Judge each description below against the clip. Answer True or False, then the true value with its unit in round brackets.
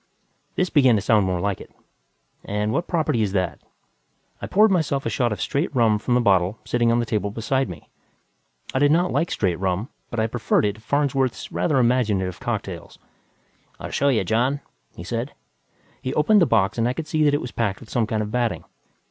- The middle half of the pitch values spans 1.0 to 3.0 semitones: False (5.0 semitones)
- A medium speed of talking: False (210 wpm)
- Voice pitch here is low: True (115 Hz)